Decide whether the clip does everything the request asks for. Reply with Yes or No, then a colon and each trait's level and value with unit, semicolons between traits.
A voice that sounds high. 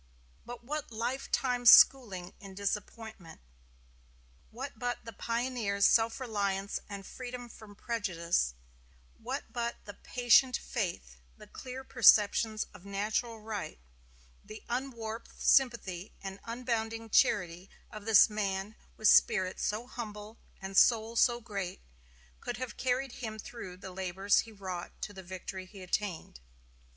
Yes: high, 215 Hz